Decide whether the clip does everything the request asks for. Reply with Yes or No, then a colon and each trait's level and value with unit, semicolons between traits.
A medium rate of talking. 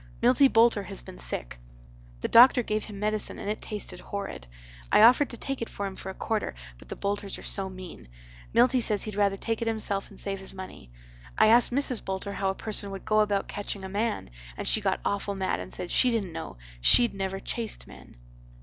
No: fast, 220 wpm